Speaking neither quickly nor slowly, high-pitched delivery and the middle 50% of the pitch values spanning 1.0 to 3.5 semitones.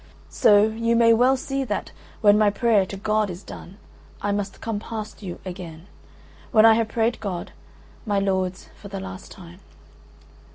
Yes: average, 170 wpm; high, 205 Hz; average, 2.7 semitones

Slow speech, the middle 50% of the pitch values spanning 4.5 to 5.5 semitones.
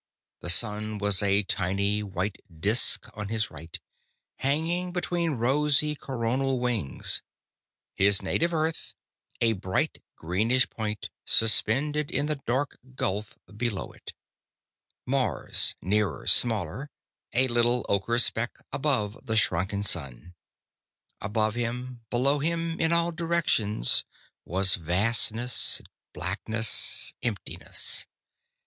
Yes: slow, 105 wpm; average, 5.2 semitones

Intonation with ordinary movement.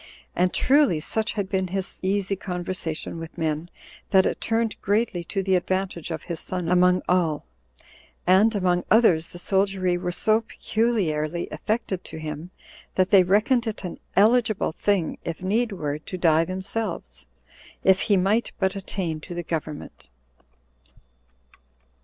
Yes: average, 3.0 semitones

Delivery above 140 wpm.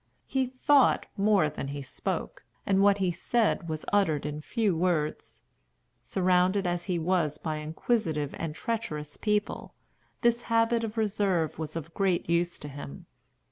Yes: average, 150 wpm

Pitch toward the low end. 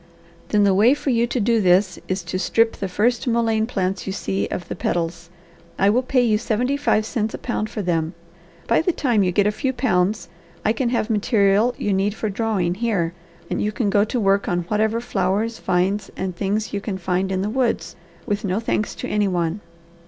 No: high, 210 Hz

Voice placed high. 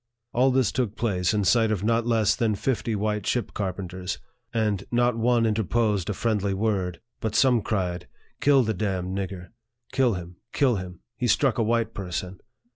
No: low, 110 Hz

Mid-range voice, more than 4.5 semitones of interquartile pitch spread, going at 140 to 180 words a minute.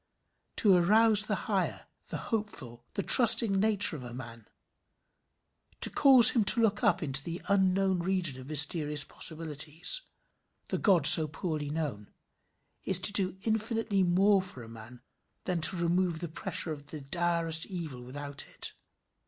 Yes: medium, 170 Hz; average, 5.2 semitones; average, 155 wpm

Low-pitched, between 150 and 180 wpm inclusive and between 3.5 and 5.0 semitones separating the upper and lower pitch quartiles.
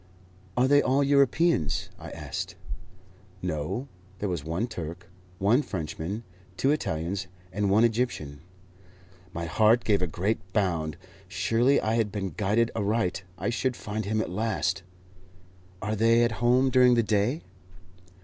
No: low, 105 Hz; average, 140 wpm; average, 4.7 semitones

